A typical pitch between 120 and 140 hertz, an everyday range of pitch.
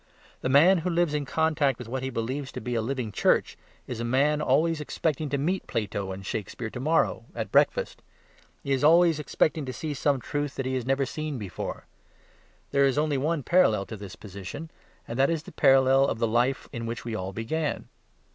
Yes: low, 135 Hz; average, 4.5 semitones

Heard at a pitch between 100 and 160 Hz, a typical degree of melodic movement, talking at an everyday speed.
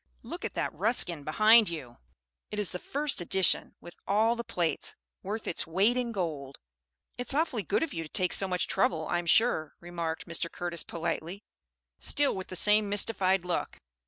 No: medium, 185 Hz; average, 4.3 semitones; average, 180 wpm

